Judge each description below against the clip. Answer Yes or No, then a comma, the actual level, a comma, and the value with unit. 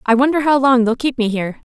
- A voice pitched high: Yes, very high, 250 Hz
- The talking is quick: Yes, fast, 280 wpm